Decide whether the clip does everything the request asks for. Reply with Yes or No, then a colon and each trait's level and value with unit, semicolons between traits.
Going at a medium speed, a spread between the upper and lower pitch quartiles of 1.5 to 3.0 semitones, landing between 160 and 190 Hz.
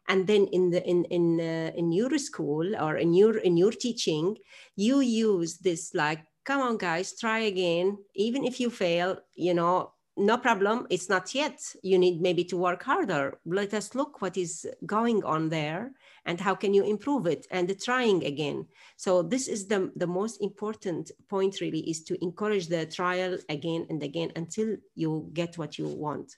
No: average, 190 wpm; average, 3.8 semitones; medium, 185 Hz